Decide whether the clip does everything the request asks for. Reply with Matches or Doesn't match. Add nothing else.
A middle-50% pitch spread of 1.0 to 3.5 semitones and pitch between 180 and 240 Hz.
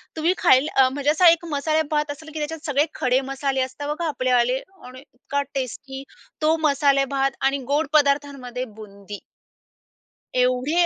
Doesn't match